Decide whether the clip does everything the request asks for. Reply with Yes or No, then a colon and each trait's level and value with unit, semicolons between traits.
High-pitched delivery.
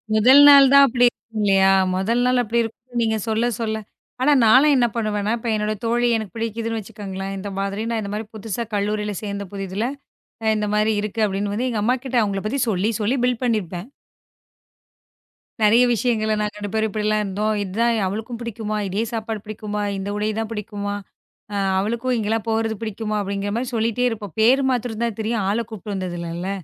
Yes: high, 215 Hz